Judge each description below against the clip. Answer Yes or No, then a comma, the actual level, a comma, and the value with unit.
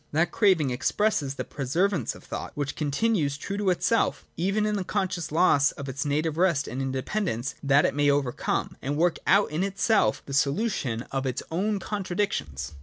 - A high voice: No, medium, 155 Hz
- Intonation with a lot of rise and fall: Yes, wide, 6.2 semitones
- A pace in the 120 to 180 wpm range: No, average, 195 wpm